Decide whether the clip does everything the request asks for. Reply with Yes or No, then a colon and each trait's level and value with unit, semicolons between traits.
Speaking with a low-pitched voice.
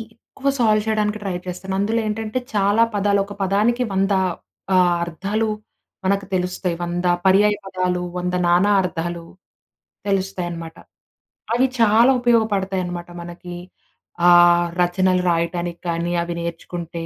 No: medium, 185 Hz